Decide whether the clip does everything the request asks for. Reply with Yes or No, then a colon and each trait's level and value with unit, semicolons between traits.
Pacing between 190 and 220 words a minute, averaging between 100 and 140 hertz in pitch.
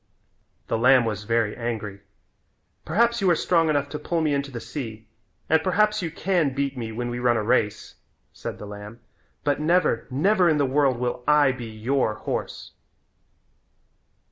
No: average, 170 wpm; low, 135 Hz